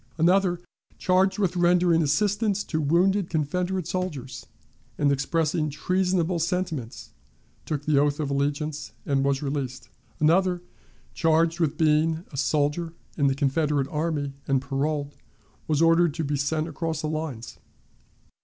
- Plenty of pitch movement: No, average, 3.5 semitones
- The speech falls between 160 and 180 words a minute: No, slow, 135 wpm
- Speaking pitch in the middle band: Yes, medium, 155 Hz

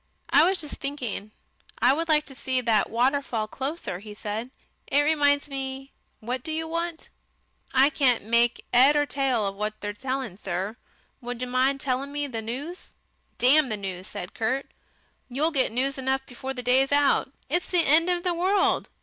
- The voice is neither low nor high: No, very high, 265 Hz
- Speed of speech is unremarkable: Yes, average, 185 wpm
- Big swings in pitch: No, average, 3.7 semitones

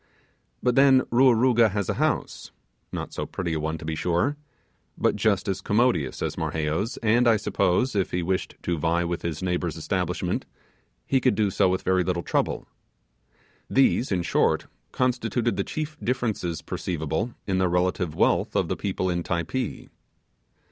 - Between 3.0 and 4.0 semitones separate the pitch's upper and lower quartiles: No, wide, 5.5 semitones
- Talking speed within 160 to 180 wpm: Yes, average, 165 wpm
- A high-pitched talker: No, very low, 95 Hz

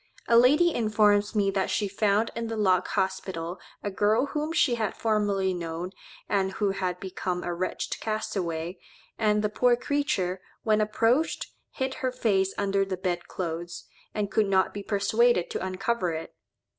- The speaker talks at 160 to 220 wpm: Yes, average, 165 wpm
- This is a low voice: No, high, 205 Hz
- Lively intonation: No, average, 3.3 semitones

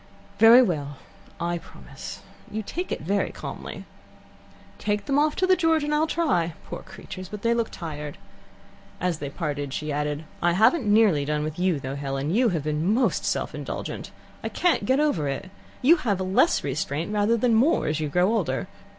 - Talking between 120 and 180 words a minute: No, average, 195 wpm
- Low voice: No, medium, 185 Hz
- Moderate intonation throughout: No, wide, 7.6 semitones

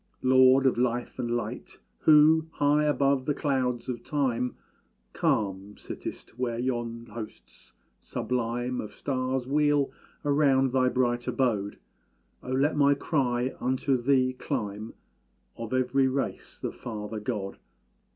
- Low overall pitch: Yes, low, 125 Hz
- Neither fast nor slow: No, slow, 125 wpm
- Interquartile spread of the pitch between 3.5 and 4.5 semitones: No, narrow, 2.5 semitones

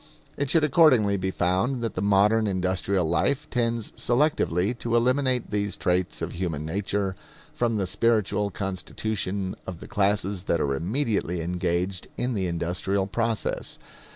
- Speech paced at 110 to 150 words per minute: Yes, average, 145 wpm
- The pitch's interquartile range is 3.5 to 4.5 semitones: Yes, average, 4.0 semitones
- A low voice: Yes, low, 100 Hz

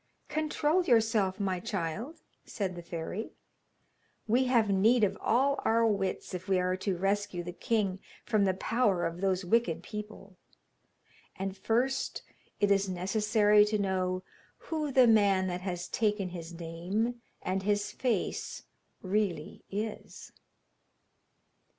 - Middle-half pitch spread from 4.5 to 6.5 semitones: No, average, 3.4 semitones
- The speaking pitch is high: Yes, high, 200 Hz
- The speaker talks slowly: Yes, slow, 130 wpm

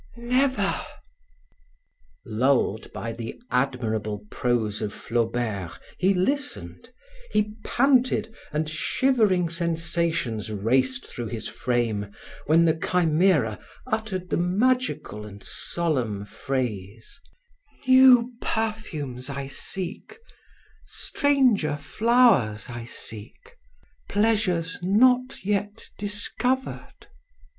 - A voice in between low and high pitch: Yes, medium, 165 Hz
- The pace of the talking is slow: Yes, slow, 85 wpm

